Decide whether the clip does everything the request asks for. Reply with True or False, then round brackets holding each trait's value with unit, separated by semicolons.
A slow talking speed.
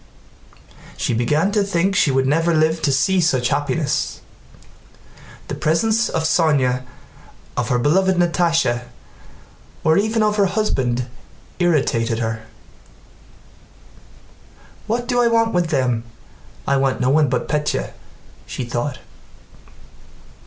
True (120 wpm)